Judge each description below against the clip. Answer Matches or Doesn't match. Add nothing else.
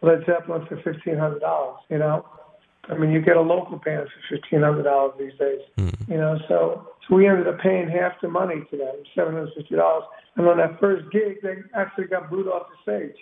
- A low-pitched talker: Doesn't match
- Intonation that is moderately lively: Matches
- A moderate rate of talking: Matches